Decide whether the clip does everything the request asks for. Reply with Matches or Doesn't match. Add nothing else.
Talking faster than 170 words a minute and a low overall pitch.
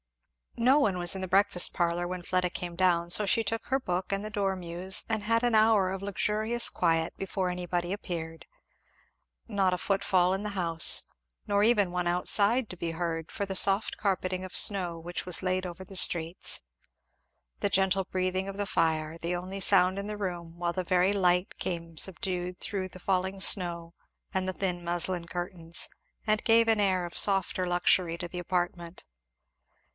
Doesn't match